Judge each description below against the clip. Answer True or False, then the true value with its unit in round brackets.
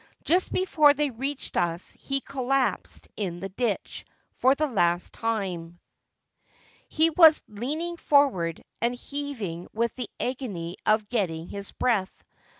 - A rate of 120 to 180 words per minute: True (135 wpm)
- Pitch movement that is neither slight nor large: False (7.1 semitones)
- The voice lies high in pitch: True (235 Hz)